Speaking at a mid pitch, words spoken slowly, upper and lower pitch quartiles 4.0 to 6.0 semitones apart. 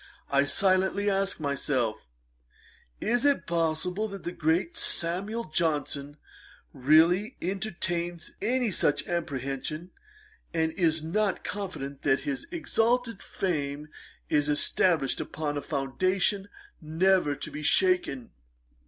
Yes: medium, 170 Hz; slow, 110 wpm; average, 5.2 semitones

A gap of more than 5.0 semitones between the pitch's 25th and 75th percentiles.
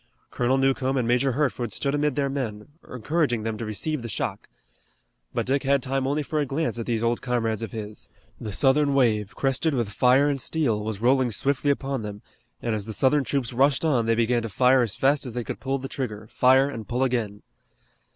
No: average, 3.4 semitones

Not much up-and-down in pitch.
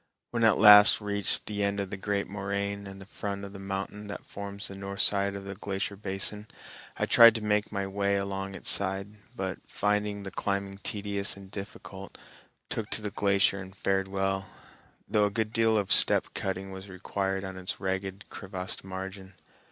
Yes: narrow, 1.0 semitones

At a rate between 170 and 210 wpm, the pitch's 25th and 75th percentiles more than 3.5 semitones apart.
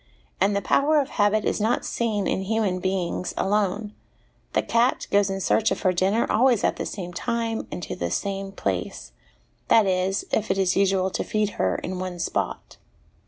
No: average, 190 wpm; average, 2.7 semitones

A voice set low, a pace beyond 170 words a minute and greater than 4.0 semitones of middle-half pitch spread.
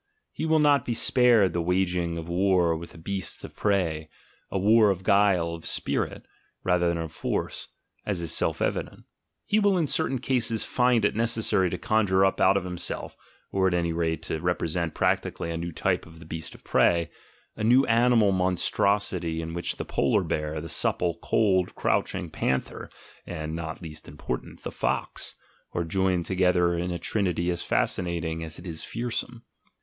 No: very low, 90 Hz; average, 185 wpm; average, 3.7 semitones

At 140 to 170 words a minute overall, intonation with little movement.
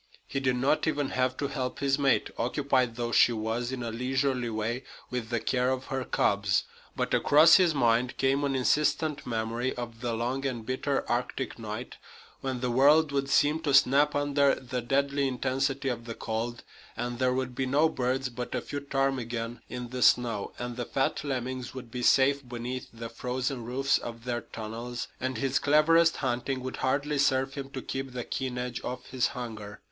No: average, 190 wpm; narrow, 2.3 semitones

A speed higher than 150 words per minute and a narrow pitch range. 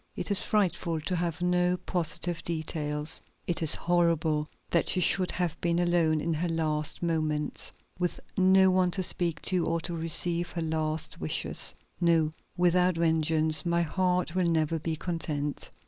Yes: average, 160 wpm; narrow, 2.1 semitones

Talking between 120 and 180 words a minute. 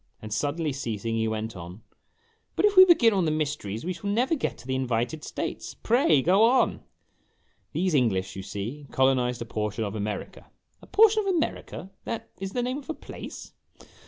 No: average, 200 wpm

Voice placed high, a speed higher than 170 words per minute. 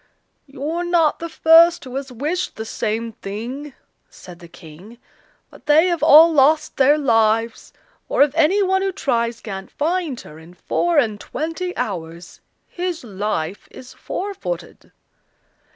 No: very high, 275 Hz; average, 145 wpm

